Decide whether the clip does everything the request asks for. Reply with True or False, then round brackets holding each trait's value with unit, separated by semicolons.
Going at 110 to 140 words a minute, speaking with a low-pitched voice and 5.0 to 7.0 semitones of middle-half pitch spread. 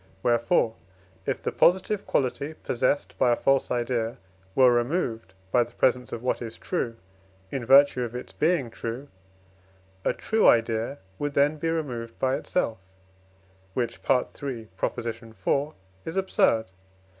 False (135 wpm; 125 Hz; 3.6 semitones)